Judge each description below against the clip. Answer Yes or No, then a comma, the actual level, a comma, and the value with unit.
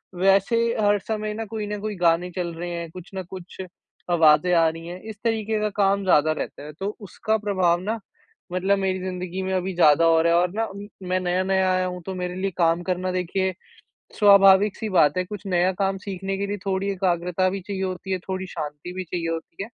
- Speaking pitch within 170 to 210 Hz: Yes, medium, 185 Hz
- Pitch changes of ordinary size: No, narrow, 2.0 semitones